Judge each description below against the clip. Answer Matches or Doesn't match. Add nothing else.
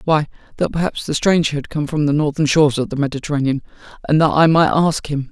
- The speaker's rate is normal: Doesn't match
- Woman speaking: Doesn't match